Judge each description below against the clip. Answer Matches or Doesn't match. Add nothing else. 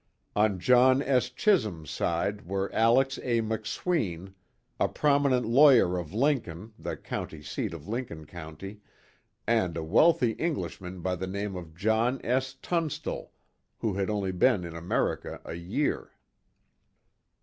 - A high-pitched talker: Doesn't match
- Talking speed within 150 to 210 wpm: Doesn't match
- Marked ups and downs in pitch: Matches